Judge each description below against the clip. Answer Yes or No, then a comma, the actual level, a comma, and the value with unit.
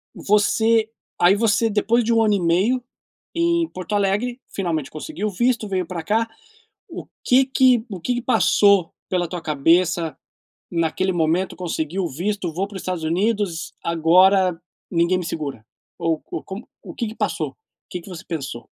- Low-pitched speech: No, high, 190 Hz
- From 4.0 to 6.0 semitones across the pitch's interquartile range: Yes, average, 4.6 semitones